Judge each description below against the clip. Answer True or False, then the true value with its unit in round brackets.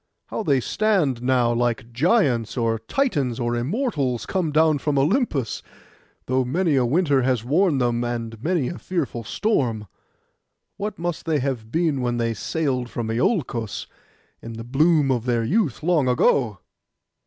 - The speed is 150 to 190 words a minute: True (155 wpm)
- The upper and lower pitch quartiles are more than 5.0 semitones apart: True (5.4 semitones)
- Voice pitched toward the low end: True (130 Hz)